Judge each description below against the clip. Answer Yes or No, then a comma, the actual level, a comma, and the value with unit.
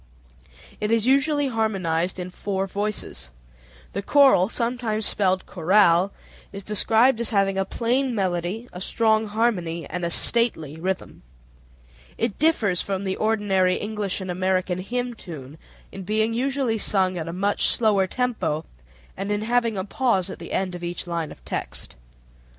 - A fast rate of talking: No, average, 155 wpm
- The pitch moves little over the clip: No, average, 3.8 semitones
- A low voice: No, high, 200 Hz